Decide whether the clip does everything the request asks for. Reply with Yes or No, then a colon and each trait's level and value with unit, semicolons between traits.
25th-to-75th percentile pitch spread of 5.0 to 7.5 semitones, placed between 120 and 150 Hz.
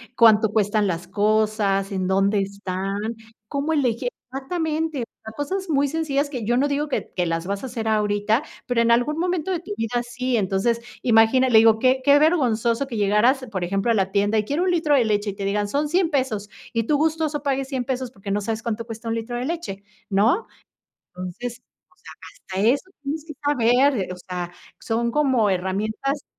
No: wide, 5.4 semitones; high, 235 Hz